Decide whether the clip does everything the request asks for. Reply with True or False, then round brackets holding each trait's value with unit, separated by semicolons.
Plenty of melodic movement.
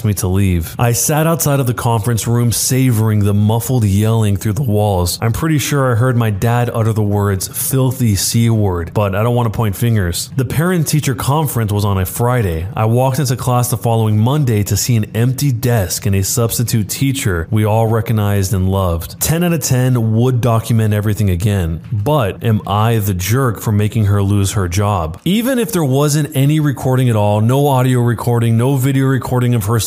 False (3.8 semitones)